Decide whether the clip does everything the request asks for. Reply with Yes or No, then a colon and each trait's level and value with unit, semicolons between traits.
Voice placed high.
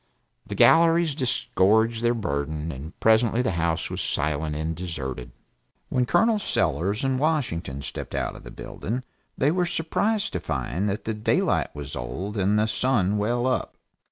No: low, 105 Hz